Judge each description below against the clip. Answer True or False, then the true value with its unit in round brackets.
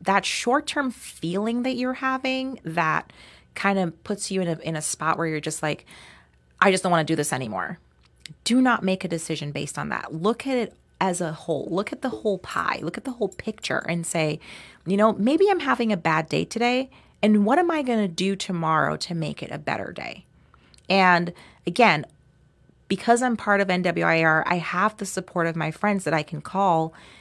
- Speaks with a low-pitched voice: False (190 Hz)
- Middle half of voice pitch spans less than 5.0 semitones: False (5.3 semitones)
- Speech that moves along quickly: True (210 wpm)